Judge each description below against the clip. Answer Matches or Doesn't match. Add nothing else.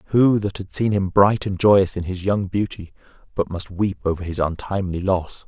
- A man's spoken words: Matches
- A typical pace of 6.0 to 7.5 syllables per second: Doesn't match